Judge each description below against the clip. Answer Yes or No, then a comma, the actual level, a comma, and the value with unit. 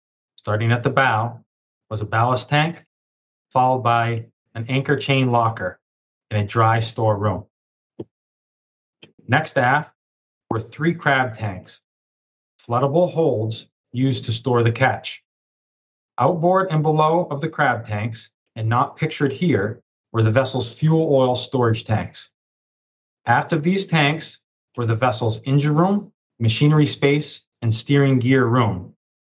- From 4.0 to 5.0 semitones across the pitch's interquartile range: Yes, average, 4.4 semitones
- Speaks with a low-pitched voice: Yes, low, 125 Hz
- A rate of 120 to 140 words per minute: Yes, slow, 135 wpm